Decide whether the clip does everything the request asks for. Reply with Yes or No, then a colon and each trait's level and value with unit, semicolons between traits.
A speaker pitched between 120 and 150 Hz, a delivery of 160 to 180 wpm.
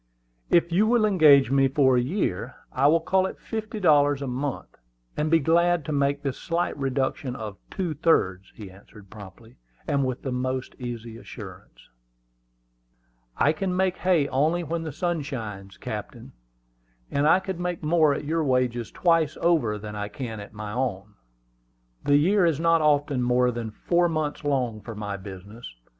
Yes: medium, 140 Hz; average, 175 wpm